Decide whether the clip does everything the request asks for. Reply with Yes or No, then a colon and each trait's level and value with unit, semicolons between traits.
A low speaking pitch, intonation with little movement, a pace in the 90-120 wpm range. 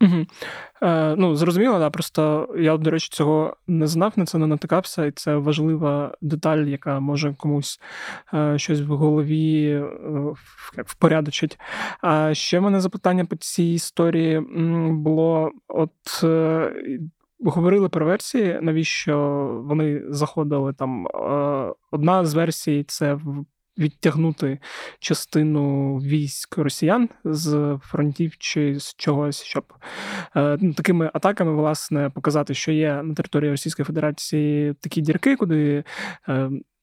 No: medium, 155 Hz; narrow, 2.2 semitones; average, 115 wpm